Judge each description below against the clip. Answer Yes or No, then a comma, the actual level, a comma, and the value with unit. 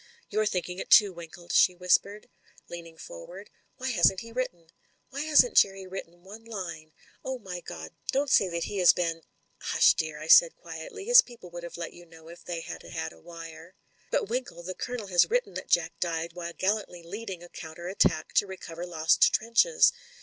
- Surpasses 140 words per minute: Yes, average, 195 wpm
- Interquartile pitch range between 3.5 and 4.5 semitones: Yes, average, 4.2 semitones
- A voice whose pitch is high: No, medium, 180 Hz